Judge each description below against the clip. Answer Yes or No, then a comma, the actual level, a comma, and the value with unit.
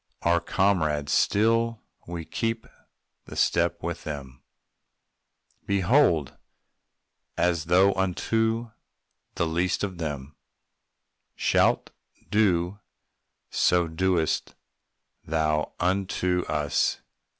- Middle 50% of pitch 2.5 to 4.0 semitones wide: Yes, average, 3.7 semitones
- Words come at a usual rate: No, slow, 85 wpm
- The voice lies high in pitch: No, very low, 90 Hz